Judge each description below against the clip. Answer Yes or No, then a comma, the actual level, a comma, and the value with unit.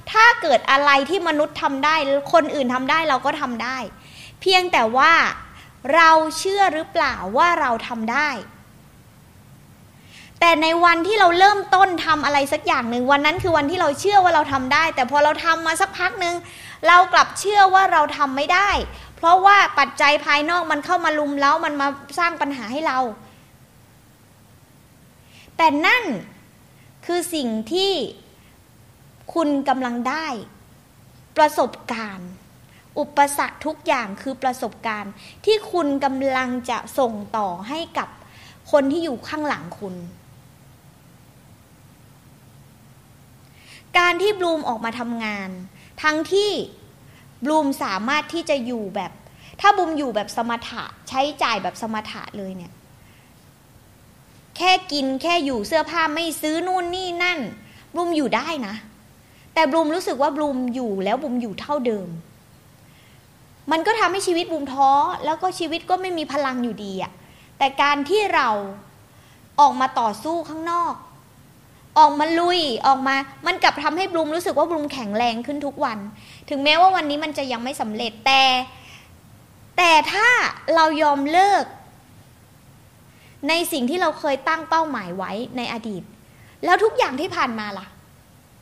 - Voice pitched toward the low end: No, very high, 290 Hz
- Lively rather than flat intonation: Yes, wide, 5.8 semitones